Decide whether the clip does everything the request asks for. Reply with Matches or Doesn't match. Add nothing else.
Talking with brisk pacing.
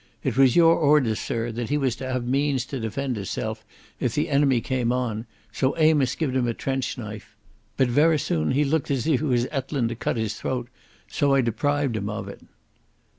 Matches